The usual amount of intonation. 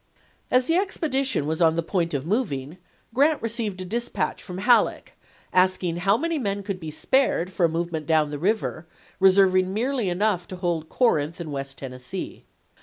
No: wide, 5.9 semitones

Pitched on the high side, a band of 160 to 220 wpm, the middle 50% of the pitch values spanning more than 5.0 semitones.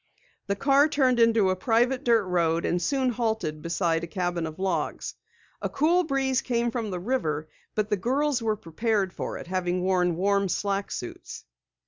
Yes: high, 200 Hz; average, 175 wpm; wide, 5.5 semitones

